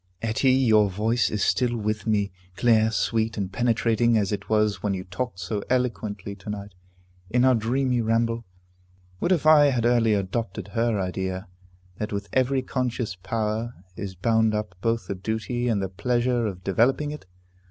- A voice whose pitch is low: Yes, low, 110 Hz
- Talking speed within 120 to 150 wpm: No, average, 170 wpm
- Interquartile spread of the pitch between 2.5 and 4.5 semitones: Yes, average, 3.0 semitones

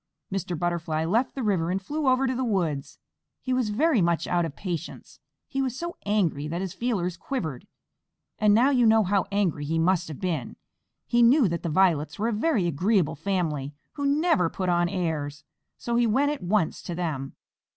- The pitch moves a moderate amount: No, wide, 6.3 semitones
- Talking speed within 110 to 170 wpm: No, average, 195 wpm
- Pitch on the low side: No, medium, 185 Hz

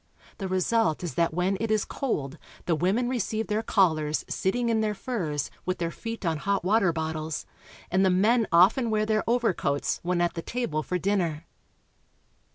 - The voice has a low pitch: No, high, 190 Hz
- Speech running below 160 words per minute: No, average, 175 wpm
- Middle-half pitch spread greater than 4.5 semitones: Yes, average, 4.9 semitones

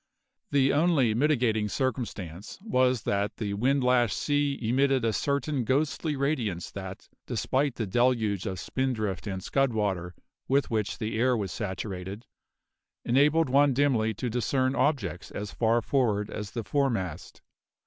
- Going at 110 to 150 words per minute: Yes, average, 140 wpm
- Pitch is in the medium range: No, low, 120 Hz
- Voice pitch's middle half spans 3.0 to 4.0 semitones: No, average, 4.8 semitones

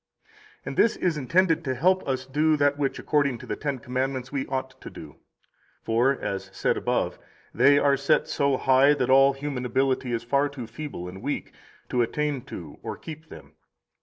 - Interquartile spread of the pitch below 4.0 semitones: Yes, narrow, 2.4 semitones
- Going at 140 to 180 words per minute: No, average, 195 wpm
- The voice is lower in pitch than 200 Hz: Yes, low, 135 Hz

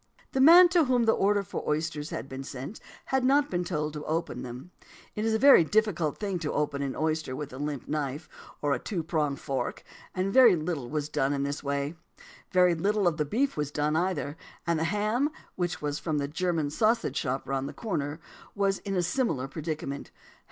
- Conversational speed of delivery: No, fast, 210 wpm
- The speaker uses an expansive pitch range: Yes, wide, 5.7 semitones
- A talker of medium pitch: Yes, medium, 160 Hz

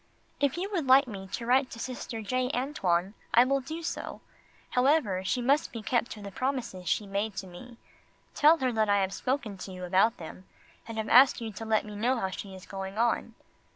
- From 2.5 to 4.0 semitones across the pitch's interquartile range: No, average, 4.7 semitones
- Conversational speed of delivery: No, fast, 220 wpm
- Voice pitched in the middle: No, high, 230 Hz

